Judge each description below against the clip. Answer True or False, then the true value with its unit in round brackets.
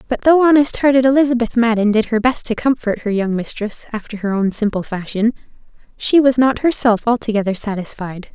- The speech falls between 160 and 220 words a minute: True (180 wpm)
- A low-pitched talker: False (230 Hz)